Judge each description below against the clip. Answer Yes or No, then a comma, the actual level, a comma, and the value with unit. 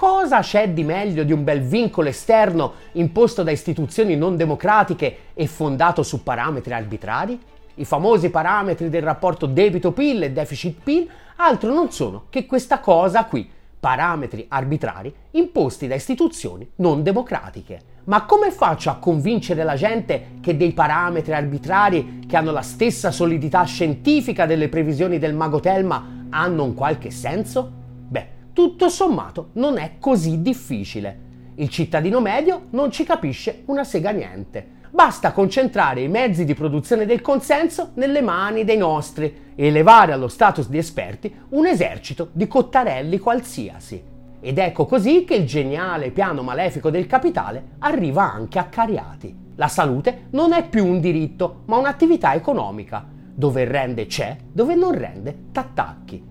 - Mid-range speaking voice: Yes, medium, 175 Hz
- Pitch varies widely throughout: Yes, wide, 7.8 semitones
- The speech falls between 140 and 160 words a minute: Yes, average, 145 wpm